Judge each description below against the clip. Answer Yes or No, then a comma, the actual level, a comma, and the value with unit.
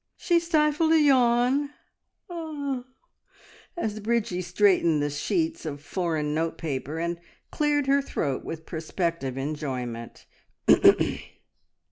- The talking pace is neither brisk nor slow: No, slow, 100 wpm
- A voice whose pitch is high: No, medium, 175 Hz